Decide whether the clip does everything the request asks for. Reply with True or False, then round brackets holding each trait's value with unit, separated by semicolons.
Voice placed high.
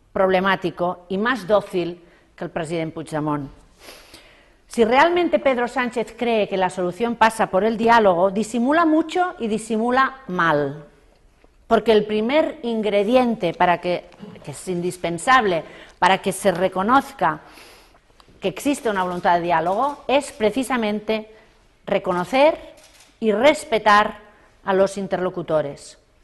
True (210 Hz)